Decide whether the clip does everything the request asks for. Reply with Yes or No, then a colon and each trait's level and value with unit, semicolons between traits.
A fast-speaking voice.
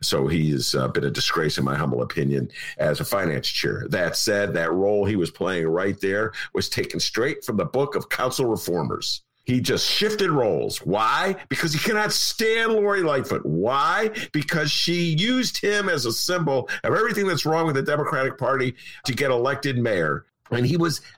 No: average, 190 wpm